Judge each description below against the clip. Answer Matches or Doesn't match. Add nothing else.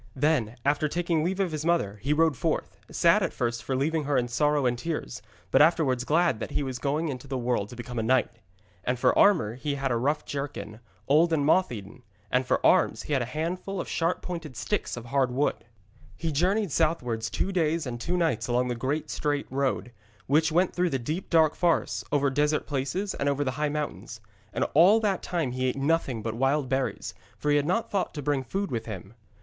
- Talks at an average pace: Doesn't match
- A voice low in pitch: Doesn't match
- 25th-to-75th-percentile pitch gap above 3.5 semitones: Matches